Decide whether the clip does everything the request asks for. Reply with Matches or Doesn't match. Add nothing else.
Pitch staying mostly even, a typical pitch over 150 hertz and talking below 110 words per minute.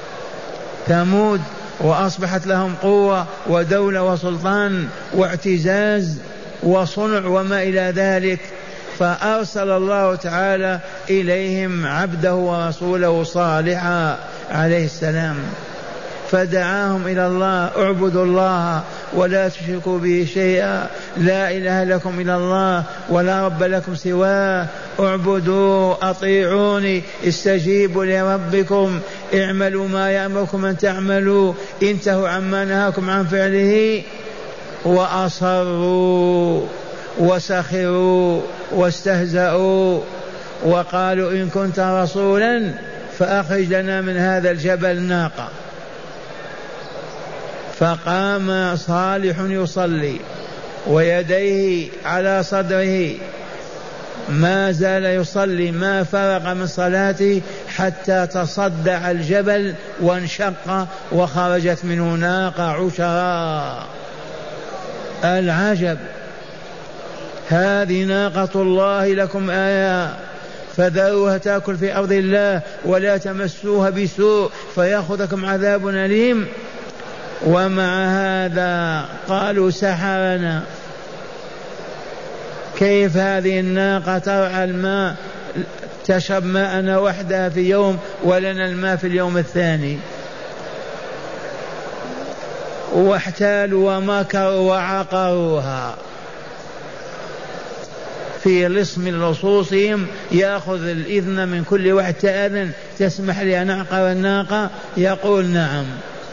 Matches